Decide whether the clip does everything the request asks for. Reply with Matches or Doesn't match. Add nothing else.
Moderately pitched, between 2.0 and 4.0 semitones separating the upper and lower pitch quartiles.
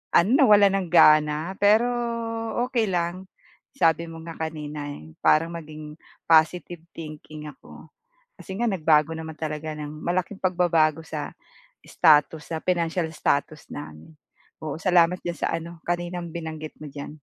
Matches